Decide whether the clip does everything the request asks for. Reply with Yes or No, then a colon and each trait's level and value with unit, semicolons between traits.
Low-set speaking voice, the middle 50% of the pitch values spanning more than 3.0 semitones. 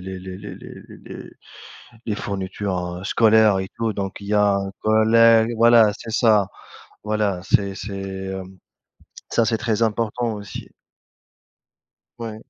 No: low, 105 Hz; narrow, 2.5 semitones